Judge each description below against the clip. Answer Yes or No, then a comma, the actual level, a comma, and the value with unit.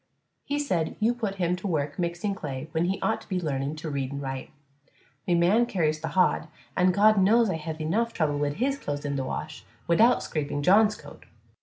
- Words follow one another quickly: Yes, fast, 210 wpm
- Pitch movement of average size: No, wide, 5.7 semitones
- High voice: No, medium, 170 Hz